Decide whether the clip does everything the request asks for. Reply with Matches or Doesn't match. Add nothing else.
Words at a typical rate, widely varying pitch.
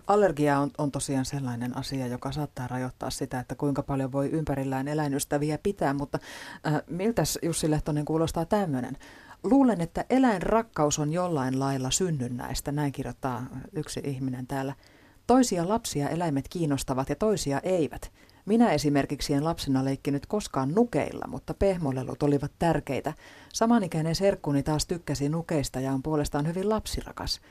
Doesn't match